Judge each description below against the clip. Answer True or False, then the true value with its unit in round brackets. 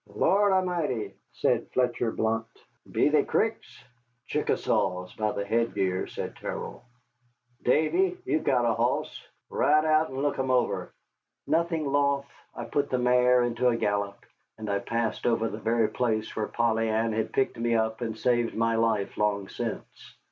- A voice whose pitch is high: False (115 Hz)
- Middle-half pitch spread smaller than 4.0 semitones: True (3.5 semitones)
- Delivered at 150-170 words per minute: True (160 wpm)